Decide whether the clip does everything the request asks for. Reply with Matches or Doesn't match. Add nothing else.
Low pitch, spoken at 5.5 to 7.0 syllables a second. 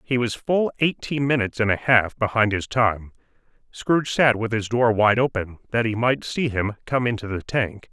Doesn't match